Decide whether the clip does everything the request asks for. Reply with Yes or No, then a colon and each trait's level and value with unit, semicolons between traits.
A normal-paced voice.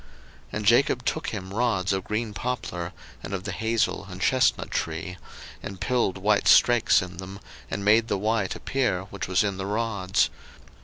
Yes: average, 175 wpm